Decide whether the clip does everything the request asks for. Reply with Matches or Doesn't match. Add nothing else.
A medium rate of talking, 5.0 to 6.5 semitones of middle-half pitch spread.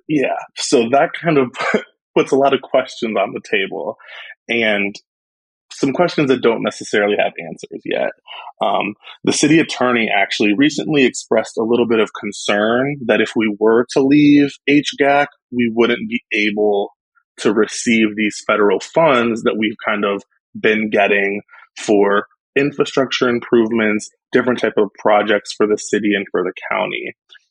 Doesn't match